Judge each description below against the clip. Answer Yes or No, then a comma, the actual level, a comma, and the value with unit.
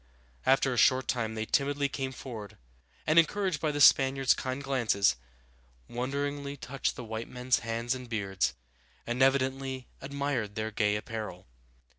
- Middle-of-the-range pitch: No, low, 130 Hz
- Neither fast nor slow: Yes, average, 145 wpm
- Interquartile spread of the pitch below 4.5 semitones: Yes, average, 3.5 semitones